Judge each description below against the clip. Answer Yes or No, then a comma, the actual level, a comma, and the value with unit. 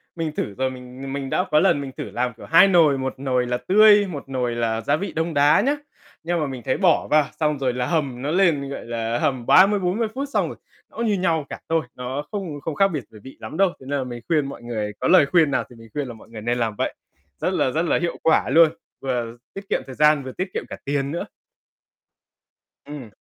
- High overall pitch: No, medium, 140 Hz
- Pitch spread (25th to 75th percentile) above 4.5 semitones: Yes, average, 5.0 semitones